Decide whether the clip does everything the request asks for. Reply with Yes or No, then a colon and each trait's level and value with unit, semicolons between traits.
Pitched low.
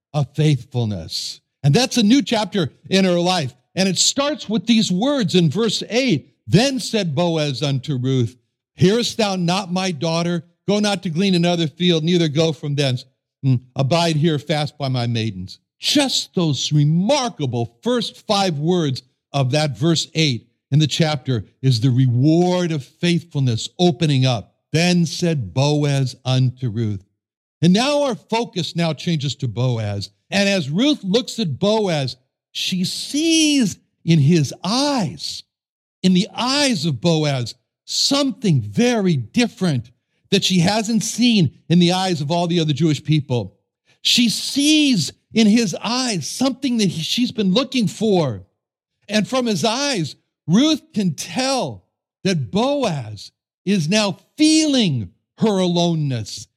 No: medium, 170 Hz